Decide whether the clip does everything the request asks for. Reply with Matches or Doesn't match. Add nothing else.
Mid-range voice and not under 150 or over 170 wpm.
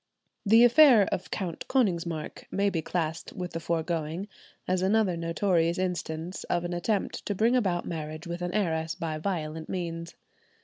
Matches